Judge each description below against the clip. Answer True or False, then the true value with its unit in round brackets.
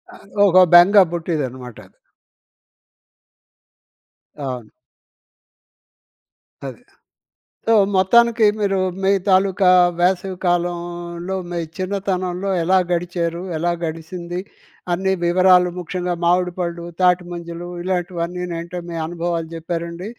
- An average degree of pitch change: False (1.6 semitones)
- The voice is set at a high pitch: False (175 Hz)